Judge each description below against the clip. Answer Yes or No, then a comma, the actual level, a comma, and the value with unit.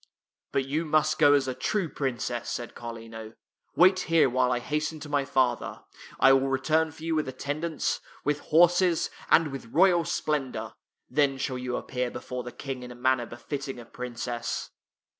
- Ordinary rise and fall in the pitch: Yes, average, 3.8 semitones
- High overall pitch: No, low, 135 Hz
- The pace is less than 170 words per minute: No, average, 180 wpm